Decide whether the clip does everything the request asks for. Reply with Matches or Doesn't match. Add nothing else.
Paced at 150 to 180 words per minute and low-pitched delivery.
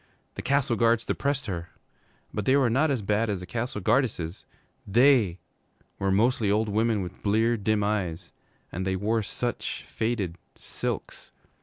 Matches